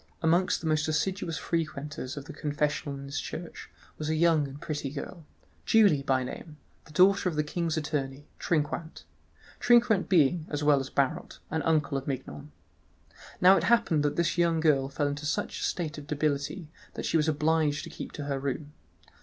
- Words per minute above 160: Yes, average, 180 wpm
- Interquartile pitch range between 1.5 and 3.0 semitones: Yes, narrow, 2.5 semitones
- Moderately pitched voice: Yes, medium, 150 Hz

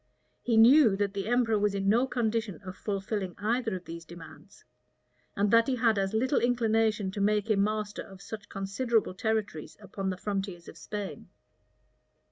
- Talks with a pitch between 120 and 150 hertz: No, high, 210 Hz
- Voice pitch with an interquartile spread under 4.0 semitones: Yes, narrow, 2.6 semitones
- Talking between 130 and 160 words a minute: No, average, 170 wpm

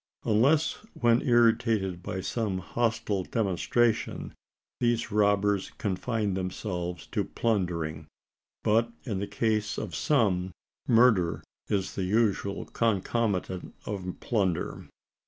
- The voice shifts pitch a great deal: No, average, 3.7 semitones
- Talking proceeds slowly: Yes, slow, 100 wpm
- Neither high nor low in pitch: No, low, 105 Hz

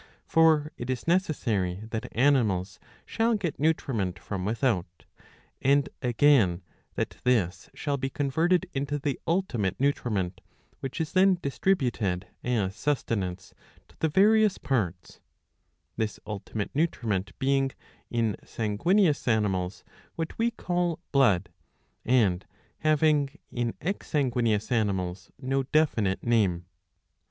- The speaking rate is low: Yes, slow, 115 wpm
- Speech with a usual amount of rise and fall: No, wide, 7.0 semitones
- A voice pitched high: No, low, 125 Hz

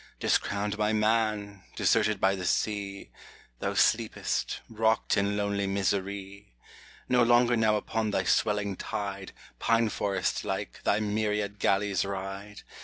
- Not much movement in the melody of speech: Yes, narrow, 1.4 semitones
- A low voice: Yes, low, 105 Hz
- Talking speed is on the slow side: Yes, slow, 125 wpm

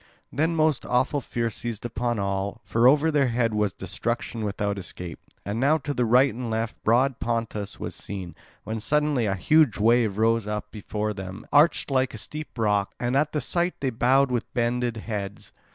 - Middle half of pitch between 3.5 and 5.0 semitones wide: Yes, average, 4.1 semitones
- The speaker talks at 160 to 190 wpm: Yes, average, 185 wpm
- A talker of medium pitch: No, low, 115 Hz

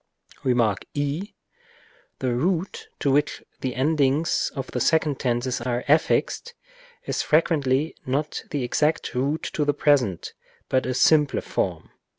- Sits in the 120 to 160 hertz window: Yes, medium, 140 Hz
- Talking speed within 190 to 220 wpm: No, slow, 135 wpm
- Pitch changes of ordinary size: Yes, average, 3.3 semitones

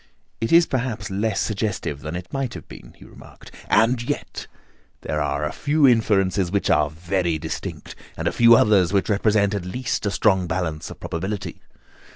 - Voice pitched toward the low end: Yes, low, 100 Hz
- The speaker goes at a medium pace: Yes, average, 180 wpm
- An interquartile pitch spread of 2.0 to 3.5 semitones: No, average, 4.4 semitones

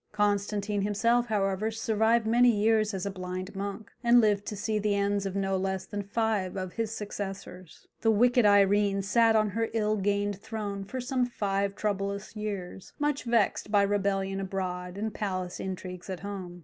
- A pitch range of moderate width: No, narrow, 2.1 semitones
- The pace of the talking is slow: No, average, 175 wpm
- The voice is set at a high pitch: Yes, high, 205 Hz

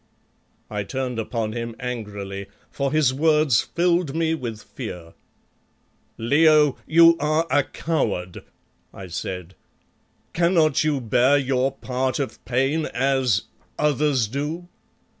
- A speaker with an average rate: No, slow, 115 wpm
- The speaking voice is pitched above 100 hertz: Yes, low, 135 Hz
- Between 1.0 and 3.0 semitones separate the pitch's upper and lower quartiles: No, average, 5.0 semitones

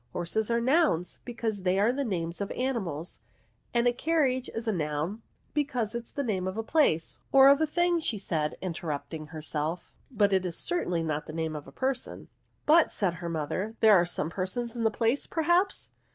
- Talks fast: Yes, fast, 210 wpm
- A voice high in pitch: Yes, high, 210 Hz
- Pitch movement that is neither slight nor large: No, wide, 7.3 semitones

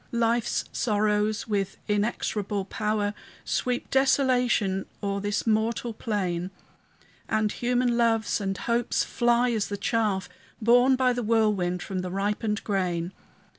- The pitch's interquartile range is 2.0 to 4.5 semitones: Yes, average, 3.0 semitones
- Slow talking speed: Yes, slow, 125 wpm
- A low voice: No, high, 215 Hz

